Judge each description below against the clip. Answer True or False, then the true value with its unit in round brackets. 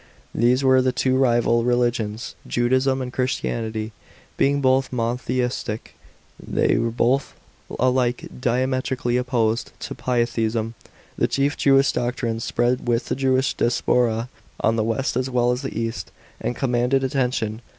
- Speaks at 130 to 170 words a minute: True (145 wpm)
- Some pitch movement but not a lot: False (1.8 semitones)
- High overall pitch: False (125 Hz)